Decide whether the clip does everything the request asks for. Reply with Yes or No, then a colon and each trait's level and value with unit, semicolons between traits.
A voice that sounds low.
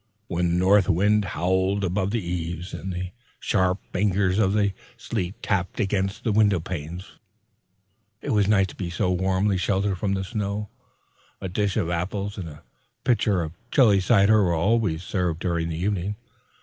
Yes: very low, 95 Hz